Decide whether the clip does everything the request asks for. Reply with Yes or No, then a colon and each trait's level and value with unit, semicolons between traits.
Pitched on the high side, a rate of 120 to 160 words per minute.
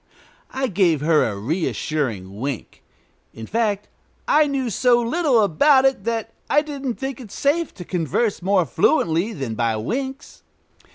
Yes: high, 205 Hz; average, 150 wpm